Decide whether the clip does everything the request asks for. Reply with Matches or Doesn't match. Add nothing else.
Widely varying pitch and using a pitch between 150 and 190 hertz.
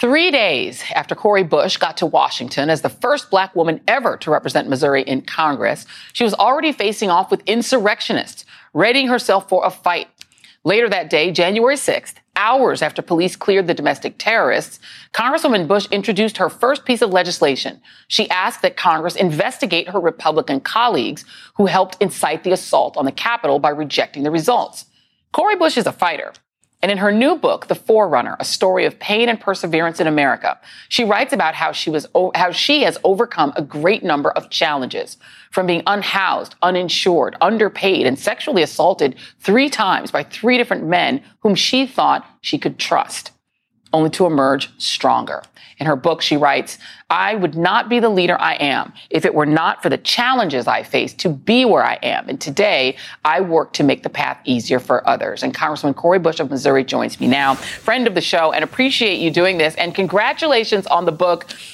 Matches